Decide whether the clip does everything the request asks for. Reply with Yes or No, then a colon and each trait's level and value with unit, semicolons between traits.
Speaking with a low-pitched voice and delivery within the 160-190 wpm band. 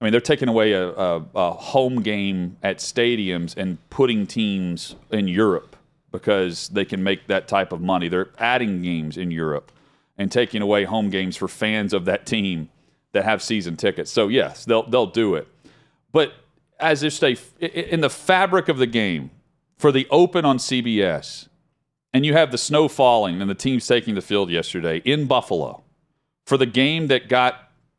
Yes: low, 120 Hz; average, 180 wpm